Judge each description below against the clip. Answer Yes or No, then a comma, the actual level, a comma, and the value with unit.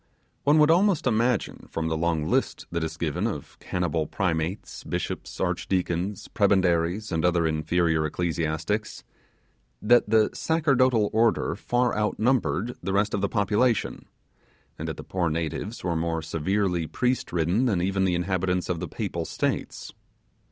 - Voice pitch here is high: No, very low, 95 Hz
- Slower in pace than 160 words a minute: Yes, average, 150 wpm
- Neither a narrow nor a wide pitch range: Yes, average, 4.7 semitones